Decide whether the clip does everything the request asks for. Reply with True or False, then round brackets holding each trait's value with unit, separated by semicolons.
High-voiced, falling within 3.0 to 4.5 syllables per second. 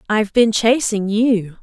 True (220 Hz; 4.3 syllables/s)